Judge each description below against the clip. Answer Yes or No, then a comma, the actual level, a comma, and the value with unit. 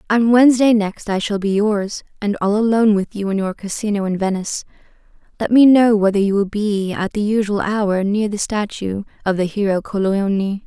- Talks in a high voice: Yes, high, 205 Hz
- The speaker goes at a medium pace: Yes, average, 195 wpm